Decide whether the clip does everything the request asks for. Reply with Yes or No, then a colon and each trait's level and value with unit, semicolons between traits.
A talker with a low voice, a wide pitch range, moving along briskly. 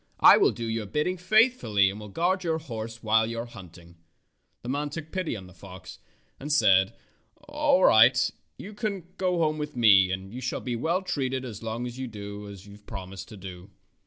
Yes: low, 115 Hz; wide, 7.9 semitones; fast, 210 wpm